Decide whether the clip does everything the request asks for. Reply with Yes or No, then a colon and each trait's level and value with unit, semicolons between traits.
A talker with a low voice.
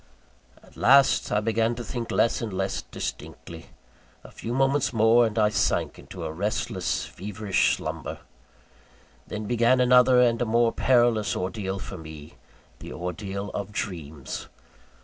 Yes: low, 110 Hz